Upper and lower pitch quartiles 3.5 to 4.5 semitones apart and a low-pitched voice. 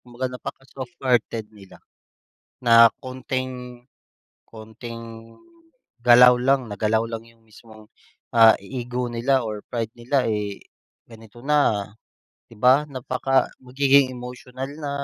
No: narrow, 2.4 semitones; low, 120 Hz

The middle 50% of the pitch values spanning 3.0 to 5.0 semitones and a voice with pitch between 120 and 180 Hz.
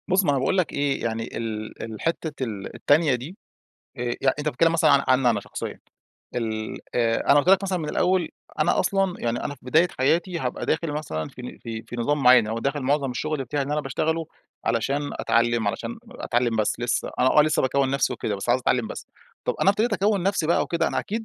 No: wide, 5.5 semitones; medium, 140 Hz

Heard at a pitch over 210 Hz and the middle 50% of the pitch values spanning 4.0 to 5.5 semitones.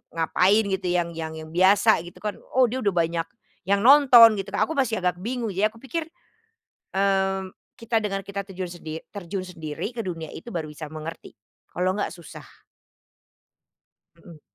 No: high, 195 Hz; average, 4.4 semitones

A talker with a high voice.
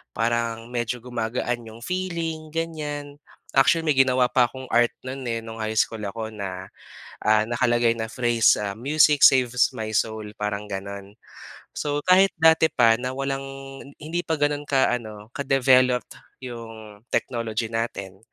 No: low, 120 Hz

